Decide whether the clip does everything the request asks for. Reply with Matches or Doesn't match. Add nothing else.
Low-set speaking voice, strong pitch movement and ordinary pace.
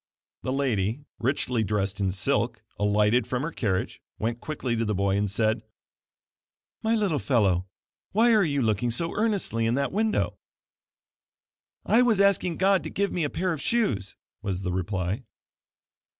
Matches